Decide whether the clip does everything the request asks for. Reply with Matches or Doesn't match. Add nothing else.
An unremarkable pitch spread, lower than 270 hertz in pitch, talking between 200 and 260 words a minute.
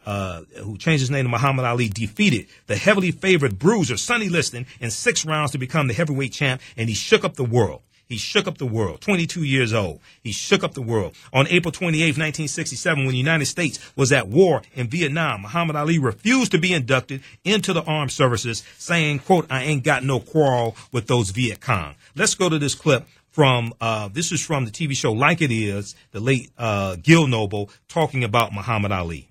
Doesn't match